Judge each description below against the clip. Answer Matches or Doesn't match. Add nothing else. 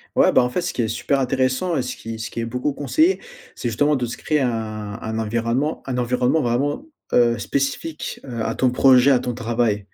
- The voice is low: Matches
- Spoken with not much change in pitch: Doesn't match